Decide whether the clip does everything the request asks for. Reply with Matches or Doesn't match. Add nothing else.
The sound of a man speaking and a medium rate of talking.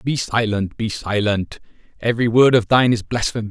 Matches